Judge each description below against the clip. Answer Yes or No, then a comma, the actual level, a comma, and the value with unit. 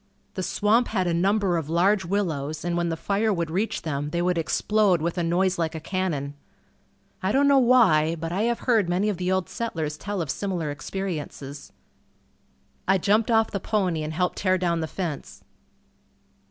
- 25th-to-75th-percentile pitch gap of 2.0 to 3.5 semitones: No, average, 3.9 semitones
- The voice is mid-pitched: Yes, medium, 180 Hz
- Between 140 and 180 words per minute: No, average, 190 wpm